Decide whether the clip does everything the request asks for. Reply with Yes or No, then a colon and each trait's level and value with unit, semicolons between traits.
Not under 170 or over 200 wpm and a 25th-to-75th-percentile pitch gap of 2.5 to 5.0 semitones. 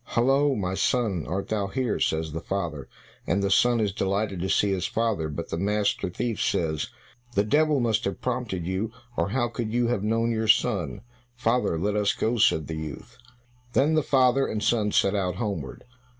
Yes: average, 195 wpm; average, 4.6 semitones